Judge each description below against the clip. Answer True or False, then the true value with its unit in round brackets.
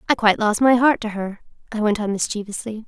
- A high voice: True (215 Hz)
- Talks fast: True (230 wpm)